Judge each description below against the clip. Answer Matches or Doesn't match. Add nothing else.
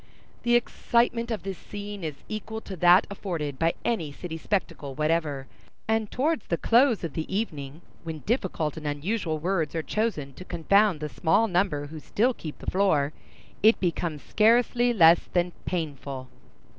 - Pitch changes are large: Matches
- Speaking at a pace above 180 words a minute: Doesn't match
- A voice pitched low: Doesn't match